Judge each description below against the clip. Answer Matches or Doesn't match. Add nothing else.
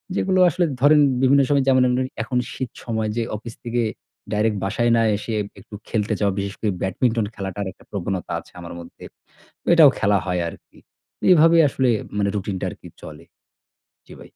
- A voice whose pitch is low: Matches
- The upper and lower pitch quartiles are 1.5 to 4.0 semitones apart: Doesn't match